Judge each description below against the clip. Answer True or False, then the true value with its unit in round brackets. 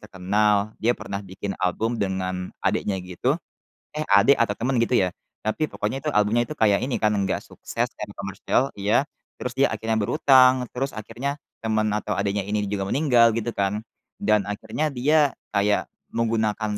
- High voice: False (110 Hz)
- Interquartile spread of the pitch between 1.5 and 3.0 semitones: False (3.6 semitones)